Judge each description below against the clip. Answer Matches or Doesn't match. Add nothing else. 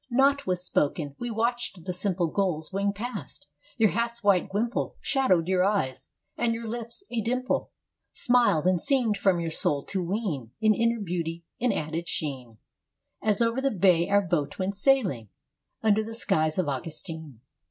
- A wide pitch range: Matches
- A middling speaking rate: Matches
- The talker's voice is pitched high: Matches